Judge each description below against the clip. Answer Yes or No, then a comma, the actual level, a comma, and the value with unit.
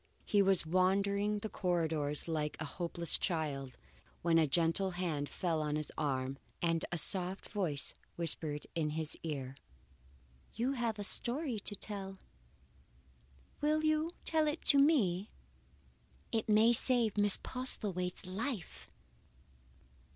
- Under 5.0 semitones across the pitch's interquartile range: No, wide, 5.4 semitones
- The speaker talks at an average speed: No, slow, 130 wpm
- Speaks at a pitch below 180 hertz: No, medium, 185 Hz